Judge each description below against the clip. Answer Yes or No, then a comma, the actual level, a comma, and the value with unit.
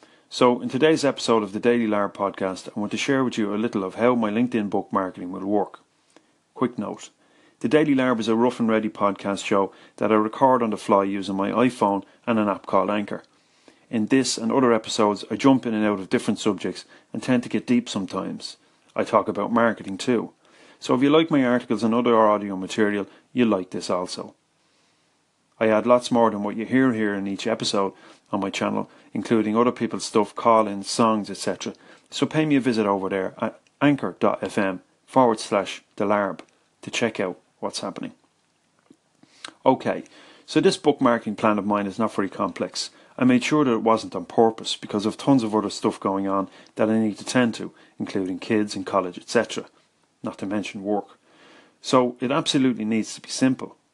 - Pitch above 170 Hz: No, low, 110 Hz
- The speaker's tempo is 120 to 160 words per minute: No, average, 195 wpm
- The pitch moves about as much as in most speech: Yes, average, 3.4 semitones